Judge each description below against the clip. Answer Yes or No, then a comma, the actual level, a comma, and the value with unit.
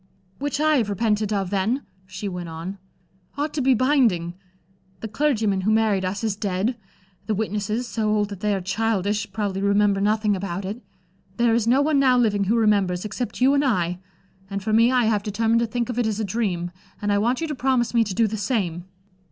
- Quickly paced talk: Yes, fast, 215 wpm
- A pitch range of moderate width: Yes, average, 3.1 semitones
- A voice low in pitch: No, high, 215 Hz